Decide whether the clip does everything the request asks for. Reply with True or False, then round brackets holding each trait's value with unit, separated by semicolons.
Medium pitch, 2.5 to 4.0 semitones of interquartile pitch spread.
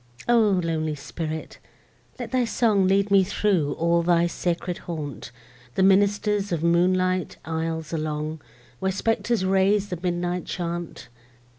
True (180 Hz; 3.3 semitones)